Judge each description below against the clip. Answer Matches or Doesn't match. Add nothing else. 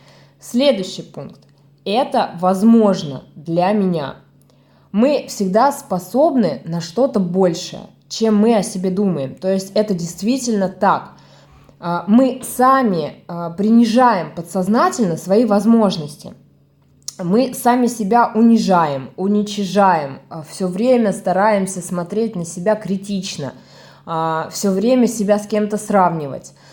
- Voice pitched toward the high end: Matches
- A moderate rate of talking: Doesn't match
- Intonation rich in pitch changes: Doesn't match